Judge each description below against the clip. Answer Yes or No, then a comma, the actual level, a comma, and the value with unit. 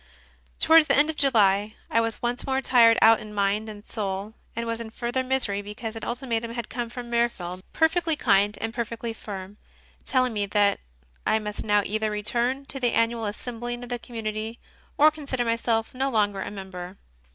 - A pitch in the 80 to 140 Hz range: No, high, 230 Hz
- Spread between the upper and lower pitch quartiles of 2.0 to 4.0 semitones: Yes, average, 2.8 semitones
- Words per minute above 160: Yes, average, 185 wpm